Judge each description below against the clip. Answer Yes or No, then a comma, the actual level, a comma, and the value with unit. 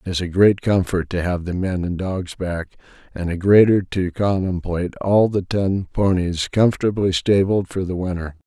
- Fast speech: No, average, 185 wpm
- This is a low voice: Yes, very low, 95 Hz